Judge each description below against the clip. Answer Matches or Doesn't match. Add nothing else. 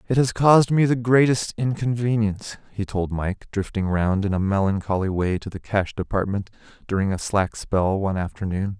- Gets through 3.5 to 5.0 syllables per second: Doesn't match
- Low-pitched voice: Matches